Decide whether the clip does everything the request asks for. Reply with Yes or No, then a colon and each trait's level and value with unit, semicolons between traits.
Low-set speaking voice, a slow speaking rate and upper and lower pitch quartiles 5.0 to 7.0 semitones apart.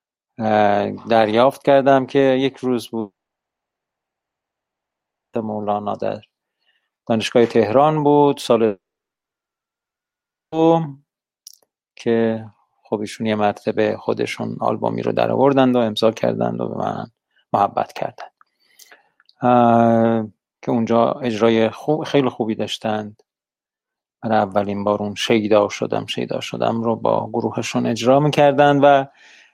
No: low, 115 Hz; slow, 100 wpm; average, 3.5 semitones